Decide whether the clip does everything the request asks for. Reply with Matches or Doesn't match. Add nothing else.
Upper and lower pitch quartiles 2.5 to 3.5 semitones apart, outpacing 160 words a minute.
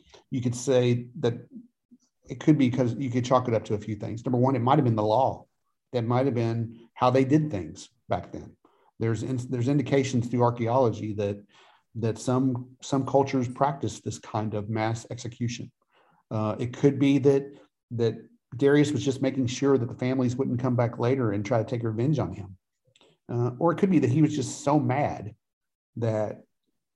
Matches